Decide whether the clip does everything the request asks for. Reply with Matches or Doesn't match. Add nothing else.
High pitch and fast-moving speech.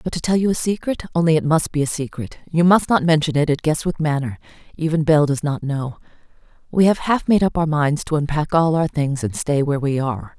Doesn't match